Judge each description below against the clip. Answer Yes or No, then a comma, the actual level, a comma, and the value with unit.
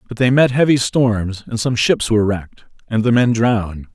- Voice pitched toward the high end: No, low, 115 Hz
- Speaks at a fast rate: Yes, fast, 215 wpm